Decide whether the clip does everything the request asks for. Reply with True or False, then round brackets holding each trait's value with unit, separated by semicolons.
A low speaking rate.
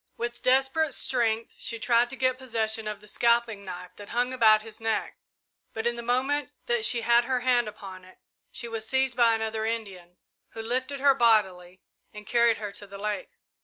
False (195 wpm)